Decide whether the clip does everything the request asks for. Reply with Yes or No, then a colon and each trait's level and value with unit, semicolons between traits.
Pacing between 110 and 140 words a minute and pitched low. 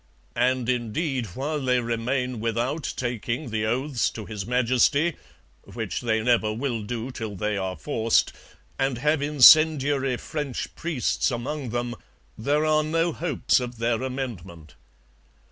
Yes: slow, 135 wpm; low, 125 Hz